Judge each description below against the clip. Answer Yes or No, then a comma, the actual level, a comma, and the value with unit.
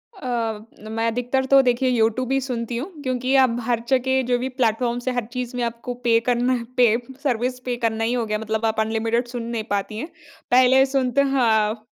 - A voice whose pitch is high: Yes, high, 245 Hz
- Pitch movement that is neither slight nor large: No, narrow, 2.1 semitones